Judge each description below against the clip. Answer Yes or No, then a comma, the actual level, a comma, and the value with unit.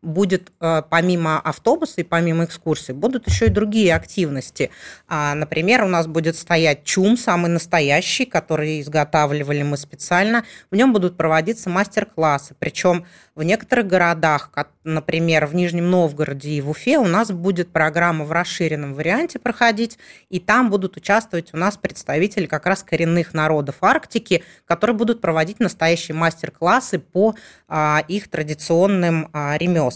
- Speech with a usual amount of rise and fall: Yes, average, 3.9 semitones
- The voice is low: No, medium, 170 Hz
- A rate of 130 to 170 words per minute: Yes, average, 135 wpm